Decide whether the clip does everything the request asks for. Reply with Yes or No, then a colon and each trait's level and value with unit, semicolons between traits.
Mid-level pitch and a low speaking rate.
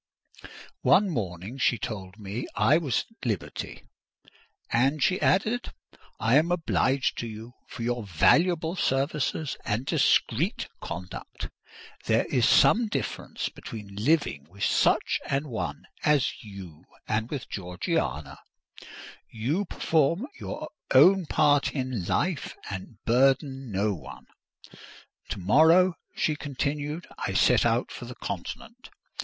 No: low, 130 Hz; slow, 125 wpm